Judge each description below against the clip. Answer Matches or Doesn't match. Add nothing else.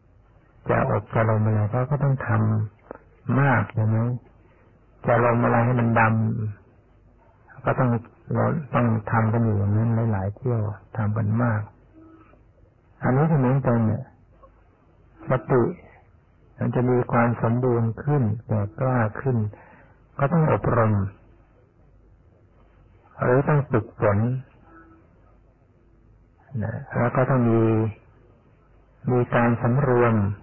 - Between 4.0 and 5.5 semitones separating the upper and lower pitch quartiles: Doesn't match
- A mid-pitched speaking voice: Doesn't match